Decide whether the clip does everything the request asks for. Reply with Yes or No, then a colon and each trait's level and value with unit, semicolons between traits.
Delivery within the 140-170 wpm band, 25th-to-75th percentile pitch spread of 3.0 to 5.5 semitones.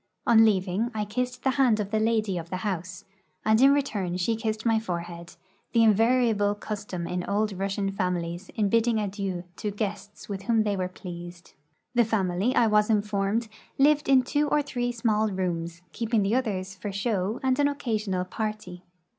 No: average, 180 wpm; average, 3.5 semitones